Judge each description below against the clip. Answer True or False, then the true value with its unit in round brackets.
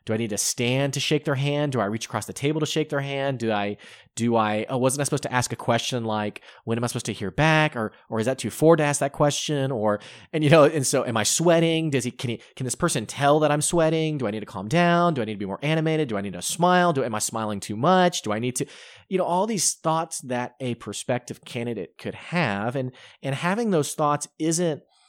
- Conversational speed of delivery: False (275 wpm)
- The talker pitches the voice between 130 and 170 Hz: True (135 Hz)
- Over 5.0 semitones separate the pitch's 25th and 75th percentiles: True (5.4 semitones)